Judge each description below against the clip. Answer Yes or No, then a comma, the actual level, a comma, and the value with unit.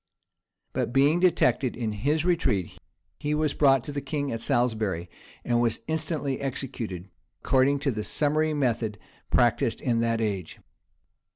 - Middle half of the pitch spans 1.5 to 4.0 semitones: No, average, 4.4 semitones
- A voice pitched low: Yes, low, 130 Hz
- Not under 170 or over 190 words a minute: No, average, 145 wpm